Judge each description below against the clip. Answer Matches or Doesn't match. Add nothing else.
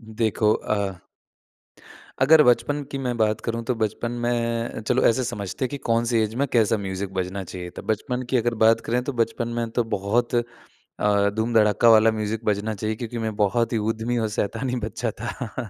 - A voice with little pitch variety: Matches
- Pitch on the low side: Matches